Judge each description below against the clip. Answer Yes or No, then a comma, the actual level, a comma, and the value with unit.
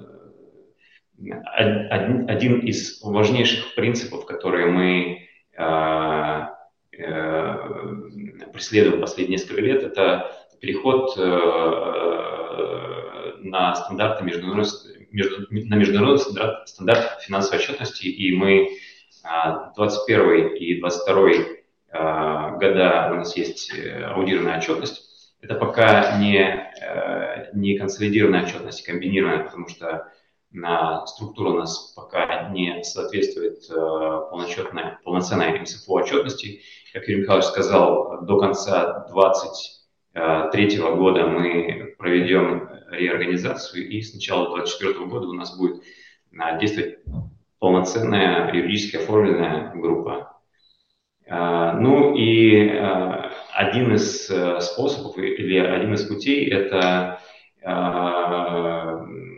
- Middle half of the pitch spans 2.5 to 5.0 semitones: Yes, average, 3.5 semitones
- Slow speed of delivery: Yes, slow, 95 wpm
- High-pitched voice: No, very low, 95 Hz